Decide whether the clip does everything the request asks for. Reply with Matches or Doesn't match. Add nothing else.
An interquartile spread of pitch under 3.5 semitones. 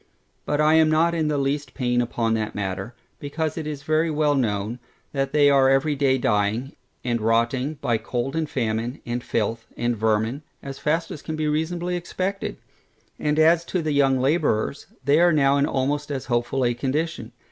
Doesn't match